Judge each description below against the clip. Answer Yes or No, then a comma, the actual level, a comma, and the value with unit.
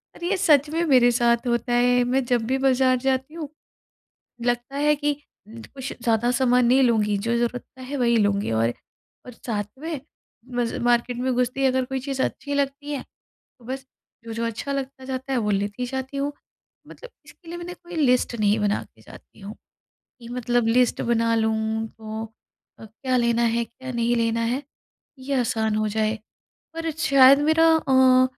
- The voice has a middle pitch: No, very high, 250 Hz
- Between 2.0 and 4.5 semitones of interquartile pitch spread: Yes, average, 2.8 semitones